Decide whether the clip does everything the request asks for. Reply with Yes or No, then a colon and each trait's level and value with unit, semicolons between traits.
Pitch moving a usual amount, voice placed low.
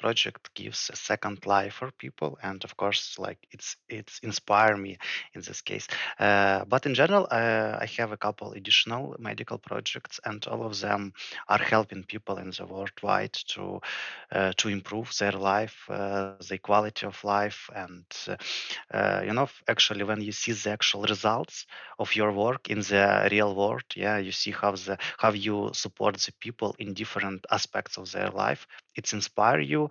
No: narrow, 1.7 semitones; low, 105 Hz